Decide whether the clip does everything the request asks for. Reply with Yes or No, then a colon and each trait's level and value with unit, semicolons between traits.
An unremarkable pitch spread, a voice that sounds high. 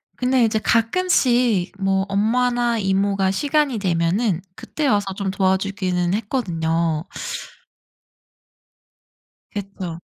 Yes: average, 4.2 semitones; high, 200 Hz